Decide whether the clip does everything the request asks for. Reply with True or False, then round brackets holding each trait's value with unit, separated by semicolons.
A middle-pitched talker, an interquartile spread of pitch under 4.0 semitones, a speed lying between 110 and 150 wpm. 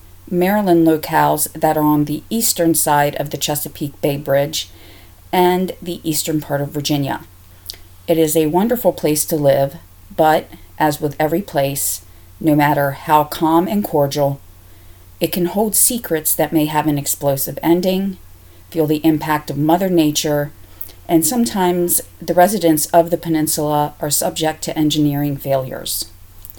True (150 Hz; 3.3 semitones; 145 wpm)